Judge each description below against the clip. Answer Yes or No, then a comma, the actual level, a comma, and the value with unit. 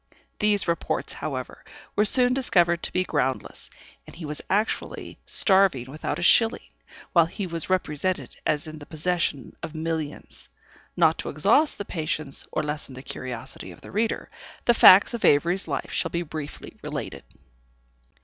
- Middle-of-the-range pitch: Yes, medium, 170 Hz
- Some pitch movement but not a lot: Yes, average, 4.5 semitones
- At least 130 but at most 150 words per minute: No, average, 160 wpm